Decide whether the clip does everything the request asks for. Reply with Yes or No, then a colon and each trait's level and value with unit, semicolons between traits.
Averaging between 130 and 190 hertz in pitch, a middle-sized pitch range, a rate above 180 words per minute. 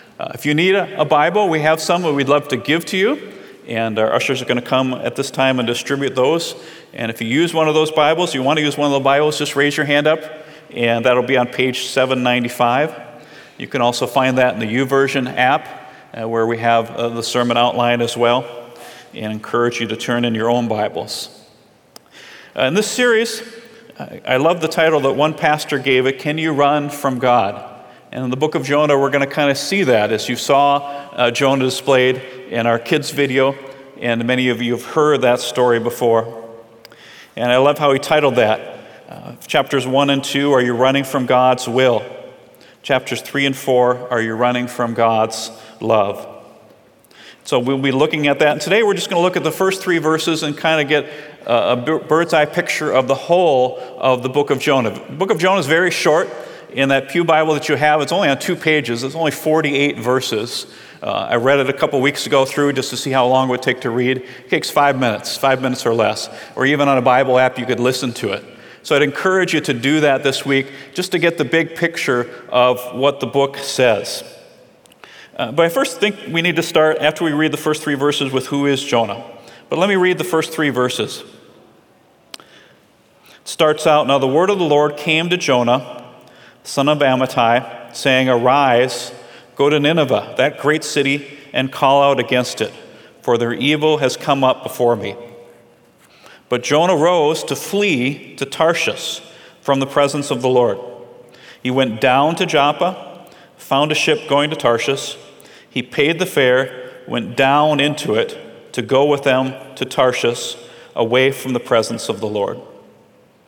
Yes: medium, 140 Hz; average, 3.7 semitones; fast, 205 wpm